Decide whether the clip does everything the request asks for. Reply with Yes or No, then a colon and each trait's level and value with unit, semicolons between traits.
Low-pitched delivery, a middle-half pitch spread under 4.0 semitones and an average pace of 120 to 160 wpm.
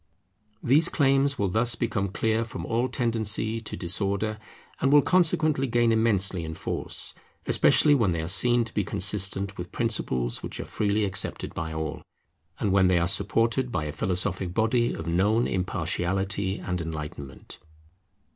No: low, 100 Hz; average, 4.4 semitones; average, 155 wpm